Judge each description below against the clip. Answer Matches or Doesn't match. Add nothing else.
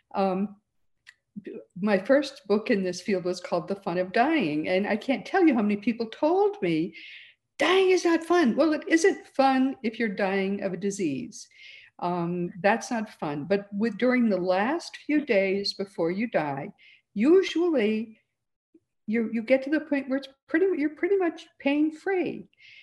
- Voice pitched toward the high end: Matches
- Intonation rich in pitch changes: Matches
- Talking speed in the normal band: Matches